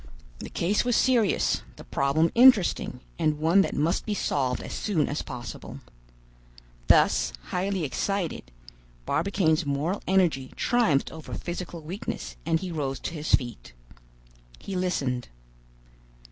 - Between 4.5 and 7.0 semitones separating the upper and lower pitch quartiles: Yes, average, 5.3 semitones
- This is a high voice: No, medium, 165 Hz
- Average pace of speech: No, slow, 130 wpm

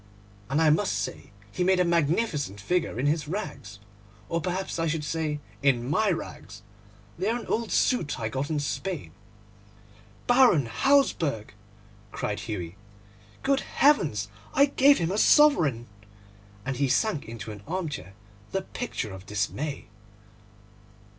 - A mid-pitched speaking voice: Yes, medium, 155 Hz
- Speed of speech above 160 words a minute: No, average, 140 wpm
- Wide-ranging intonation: Yes, wide, 8.1 semitones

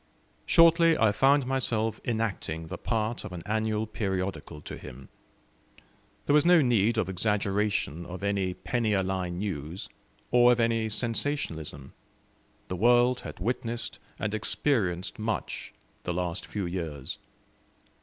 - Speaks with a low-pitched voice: Yes, low, 105 Hz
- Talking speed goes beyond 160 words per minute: No, slow, 135 wpm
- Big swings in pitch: No, average, 4.8 semitones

